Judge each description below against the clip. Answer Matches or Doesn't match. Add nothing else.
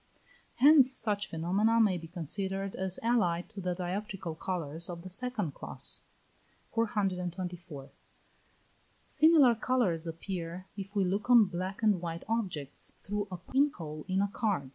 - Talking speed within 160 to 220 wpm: Doesn't match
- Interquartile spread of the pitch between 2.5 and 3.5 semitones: Doesn't match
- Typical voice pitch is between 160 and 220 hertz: Matches